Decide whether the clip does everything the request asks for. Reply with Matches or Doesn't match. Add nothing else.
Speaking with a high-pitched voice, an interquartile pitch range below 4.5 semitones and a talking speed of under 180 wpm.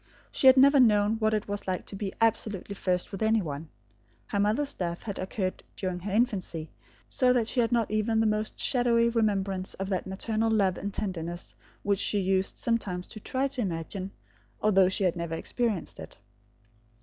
Doesn't match